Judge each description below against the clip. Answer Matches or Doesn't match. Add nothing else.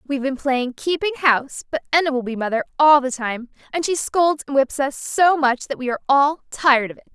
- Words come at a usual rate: Doesn't match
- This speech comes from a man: Doesn't match